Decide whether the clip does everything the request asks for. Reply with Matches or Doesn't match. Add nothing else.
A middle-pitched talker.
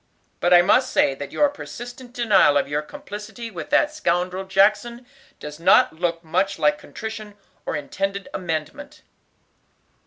Doesn't match